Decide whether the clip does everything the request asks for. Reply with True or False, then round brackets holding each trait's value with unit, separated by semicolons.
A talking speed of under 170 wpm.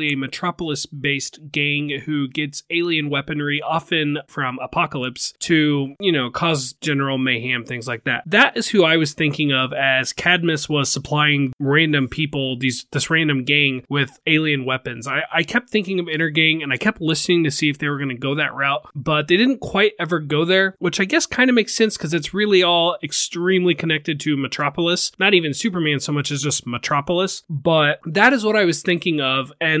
False (200 wpm)